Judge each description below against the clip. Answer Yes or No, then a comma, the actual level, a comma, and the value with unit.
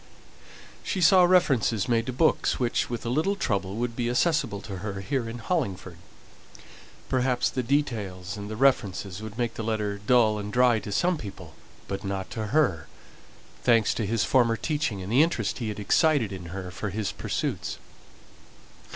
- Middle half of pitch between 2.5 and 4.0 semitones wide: No, average, 4.4 semitones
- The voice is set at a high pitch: No, low, 115 Hz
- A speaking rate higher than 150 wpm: Yes, average, 175 wpm